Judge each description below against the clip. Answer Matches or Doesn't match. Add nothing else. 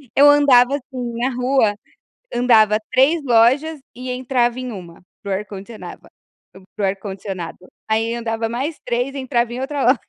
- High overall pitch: Matches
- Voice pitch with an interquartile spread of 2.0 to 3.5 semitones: Matches